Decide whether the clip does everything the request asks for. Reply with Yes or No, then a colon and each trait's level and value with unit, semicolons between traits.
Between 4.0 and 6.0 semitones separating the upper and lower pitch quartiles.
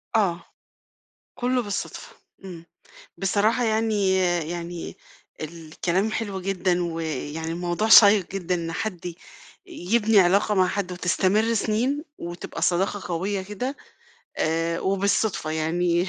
No: average, 3.5 semitones